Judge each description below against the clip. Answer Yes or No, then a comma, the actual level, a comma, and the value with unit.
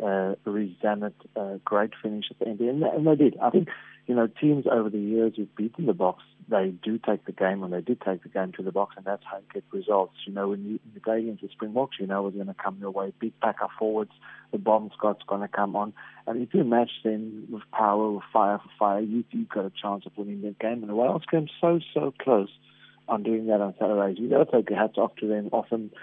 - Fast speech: Yes, fast, 260 wpm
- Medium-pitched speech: No, low, 105 Hz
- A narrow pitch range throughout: Yes, narrow, 2.1 semitones